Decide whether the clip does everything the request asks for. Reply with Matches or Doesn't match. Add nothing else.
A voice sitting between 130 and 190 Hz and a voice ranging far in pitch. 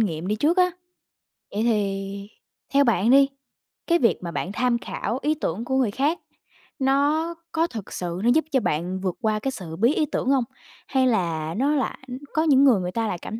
Doesn't match